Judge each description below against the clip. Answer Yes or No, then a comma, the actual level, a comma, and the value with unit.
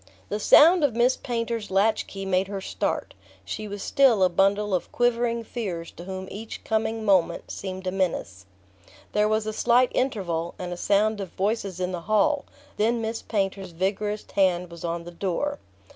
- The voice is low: No, high, 200 Hz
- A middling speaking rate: Yes, average, 185 wpm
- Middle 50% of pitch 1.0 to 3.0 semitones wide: No, average, 3.4 semitones